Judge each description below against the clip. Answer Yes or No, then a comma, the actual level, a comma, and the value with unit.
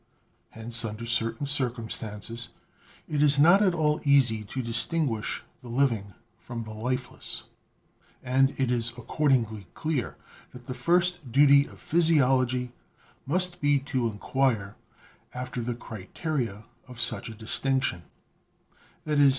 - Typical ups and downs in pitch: Yes, average, 3.9 semitones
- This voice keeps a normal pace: No, slow, 125 wpm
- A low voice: Yes, low, 125 Hz